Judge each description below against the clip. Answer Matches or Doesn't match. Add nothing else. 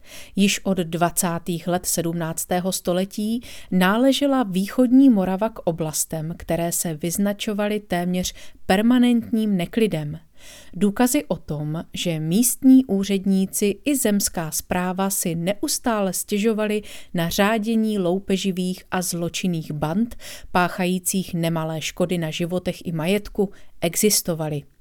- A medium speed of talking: Doesn't match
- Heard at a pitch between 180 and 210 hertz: Matches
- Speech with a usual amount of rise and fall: Matches